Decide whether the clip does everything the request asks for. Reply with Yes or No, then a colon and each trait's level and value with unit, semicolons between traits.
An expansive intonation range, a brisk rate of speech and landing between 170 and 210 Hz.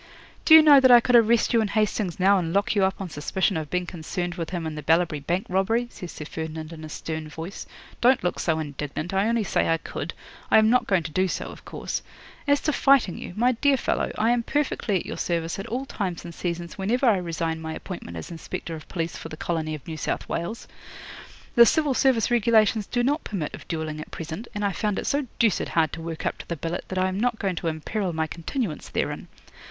Yes: wide, 5.7 semitones; fast, 240 wpm; medium, 185 Hz